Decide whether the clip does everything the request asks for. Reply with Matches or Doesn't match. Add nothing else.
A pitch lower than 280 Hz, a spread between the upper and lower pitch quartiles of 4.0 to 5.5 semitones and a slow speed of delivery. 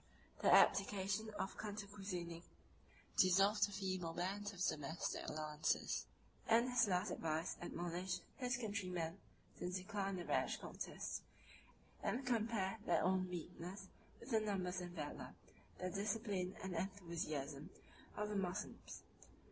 Doesn't match